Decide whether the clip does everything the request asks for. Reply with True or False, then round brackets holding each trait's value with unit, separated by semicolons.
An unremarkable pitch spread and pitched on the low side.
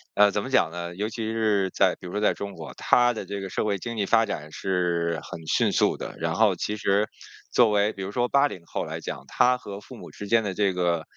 True (3.5 semitones; 100 Hz)